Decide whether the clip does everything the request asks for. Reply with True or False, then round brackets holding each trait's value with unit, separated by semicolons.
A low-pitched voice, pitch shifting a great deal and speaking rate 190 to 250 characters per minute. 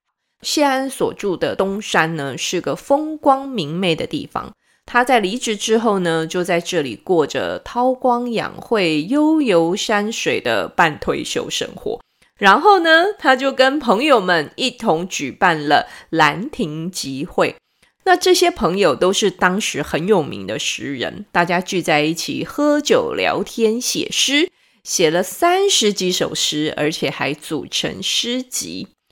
False (220 Hz; 7.8 semitones; 210 characters per minute)